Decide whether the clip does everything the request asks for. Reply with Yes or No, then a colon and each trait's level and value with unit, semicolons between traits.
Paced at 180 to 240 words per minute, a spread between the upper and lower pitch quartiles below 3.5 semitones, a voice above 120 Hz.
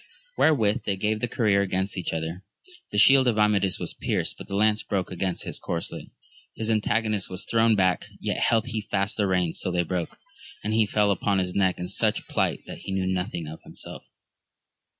No: average, 200 wpm; average, 2.8 semitones; low, 100 Hz